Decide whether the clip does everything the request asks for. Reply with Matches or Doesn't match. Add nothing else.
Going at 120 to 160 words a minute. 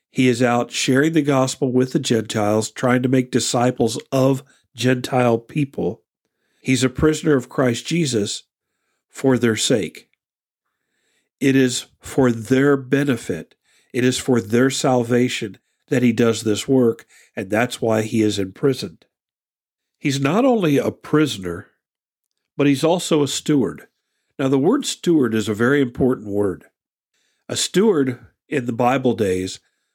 Matches